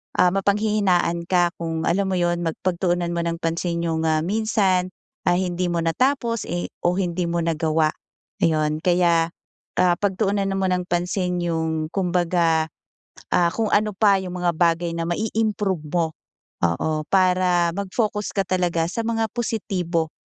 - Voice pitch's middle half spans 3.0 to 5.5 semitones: No, narrow, 2.5 semitones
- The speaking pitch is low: No, medium, 175 Hz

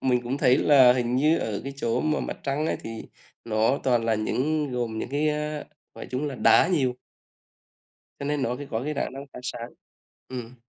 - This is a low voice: Yes, low, 130 Hz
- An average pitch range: Yes, average, 3.4 semitones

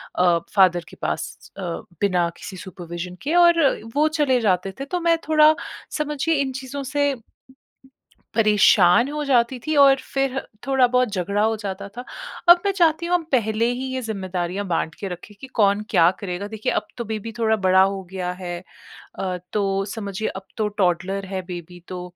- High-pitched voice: Yes, high, 210 Hz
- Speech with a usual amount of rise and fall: No, wide, 6.4 semitones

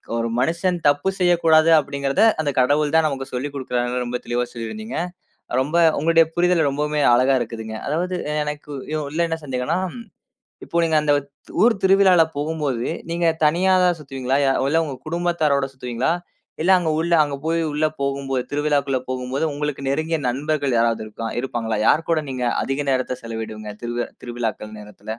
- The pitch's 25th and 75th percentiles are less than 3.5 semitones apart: No, average, 4.4 semitones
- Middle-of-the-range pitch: Yes, medium, 145 Hz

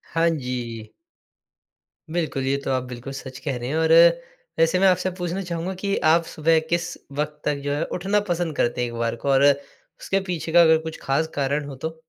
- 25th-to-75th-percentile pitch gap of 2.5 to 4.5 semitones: Yes, average, 4.0 semitones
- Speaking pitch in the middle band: Yes, medium, 160 Hz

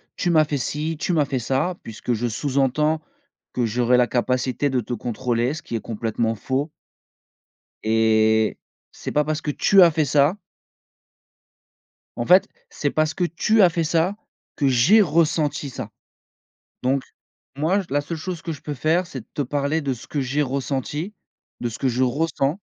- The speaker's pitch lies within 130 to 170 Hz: Yes, medium, 140 Hz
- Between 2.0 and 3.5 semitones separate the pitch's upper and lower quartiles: No, average, 4.2 semitones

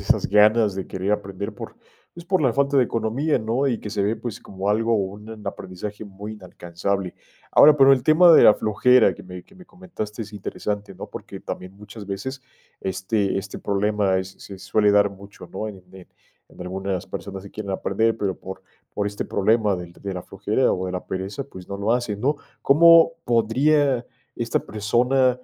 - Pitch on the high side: No, low, 105 Hz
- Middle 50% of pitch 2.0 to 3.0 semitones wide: No, average, 3.7 semitones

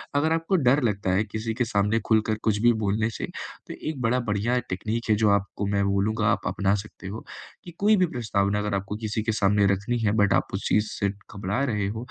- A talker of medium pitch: No, low, 110 Hz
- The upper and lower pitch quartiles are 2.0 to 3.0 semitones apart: Yes, narrow, 2.6 semitones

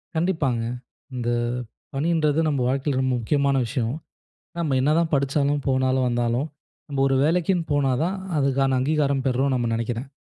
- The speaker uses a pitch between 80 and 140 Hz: Yes, low, 135 Hz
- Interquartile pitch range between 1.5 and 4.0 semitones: Yes, average, 2.7 semitones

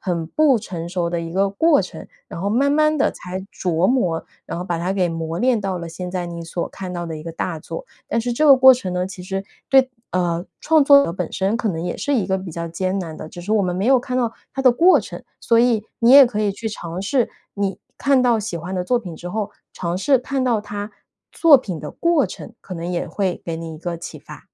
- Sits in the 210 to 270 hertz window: No, high, 195 Hz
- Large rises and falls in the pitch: Yes, wide, 6.2 semitones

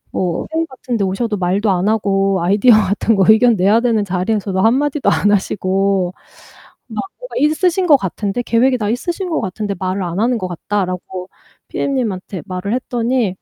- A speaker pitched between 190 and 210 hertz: Yes, high, 205 Hz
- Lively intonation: No, average, 4.5 semitones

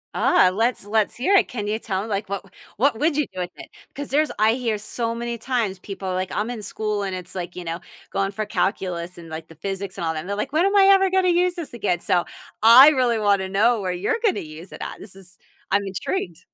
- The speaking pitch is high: Yes, high, 205 Hz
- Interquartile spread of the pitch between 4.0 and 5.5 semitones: Yes, average, 4.7 semitones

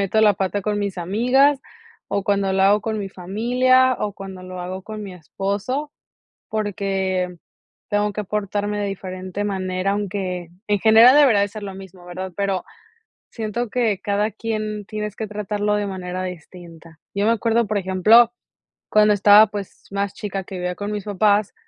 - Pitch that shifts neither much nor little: No, narrow, 2.1 semitones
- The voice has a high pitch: Yes, high, 205 Hz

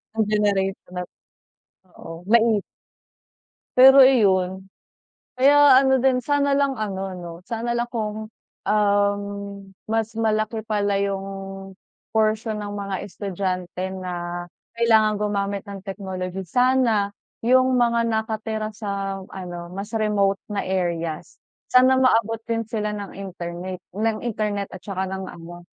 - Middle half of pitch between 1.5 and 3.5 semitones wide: Yes, average, 2.9 semitones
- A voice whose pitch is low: No, high, 210 Hz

